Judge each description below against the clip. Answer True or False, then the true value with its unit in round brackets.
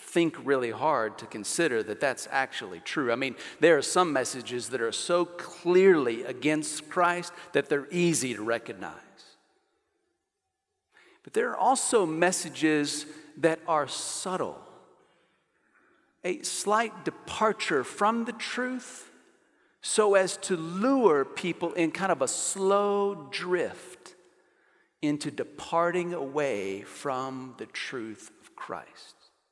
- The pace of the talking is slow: True (120 wpm)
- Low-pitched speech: False (175 Hz)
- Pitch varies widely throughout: True (6.3 semitones)